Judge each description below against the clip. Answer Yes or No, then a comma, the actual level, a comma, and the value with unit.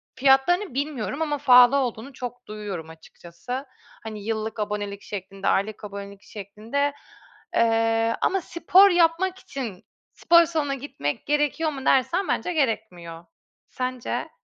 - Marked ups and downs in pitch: Yes, wide, 5.8 semitones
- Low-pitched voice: No, high, 245 Hz